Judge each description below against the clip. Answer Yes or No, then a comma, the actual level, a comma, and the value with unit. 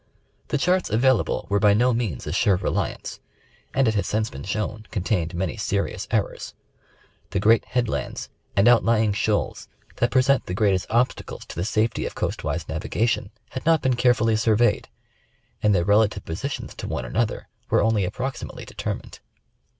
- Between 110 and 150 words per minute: No, average, 170 wpm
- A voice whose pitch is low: Yes, low, 110 Hz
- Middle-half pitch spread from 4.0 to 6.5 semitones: No, average, 3.3 semitones